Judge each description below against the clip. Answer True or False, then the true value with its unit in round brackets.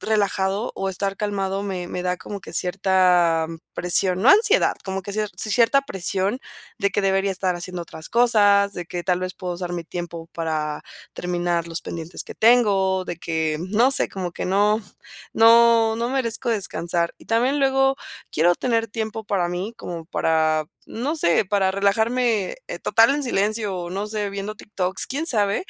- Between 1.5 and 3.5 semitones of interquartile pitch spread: False (3.9 semitones)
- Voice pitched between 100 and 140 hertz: False (195 Hz)